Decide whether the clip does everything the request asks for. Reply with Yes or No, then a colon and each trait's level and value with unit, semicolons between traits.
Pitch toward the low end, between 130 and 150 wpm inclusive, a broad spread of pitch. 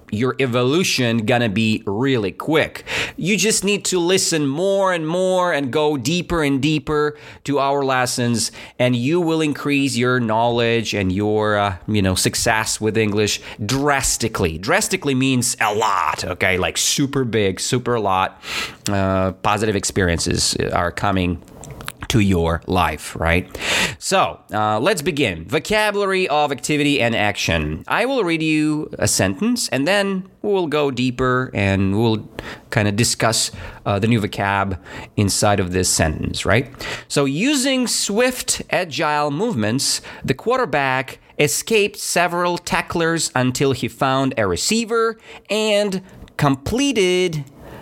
Yes: low, 130 Hz; slow, 135 wpm; wide, 7.4 semitones